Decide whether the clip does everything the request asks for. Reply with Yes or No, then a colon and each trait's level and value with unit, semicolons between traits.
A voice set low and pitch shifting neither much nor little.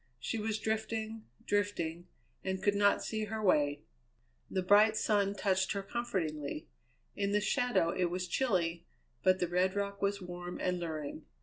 No: high, 195 Hz; average, 3.0 semitones